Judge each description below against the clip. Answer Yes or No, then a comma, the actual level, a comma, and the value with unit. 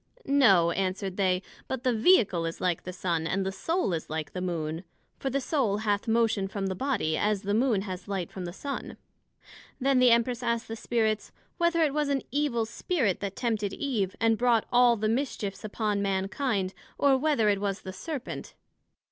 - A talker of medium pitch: No, high, 215 Hz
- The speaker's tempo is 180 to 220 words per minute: Yes, average, 190 wpm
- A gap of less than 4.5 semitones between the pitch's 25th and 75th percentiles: No, average, 4.9 semitones